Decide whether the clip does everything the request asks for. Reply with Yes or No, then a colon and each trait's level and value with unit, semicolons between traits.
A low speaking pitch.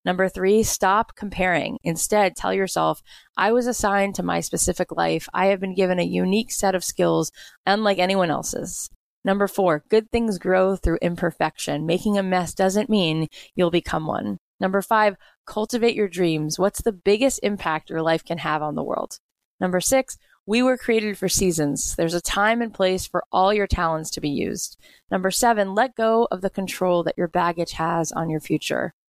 No: medium, 185 Hz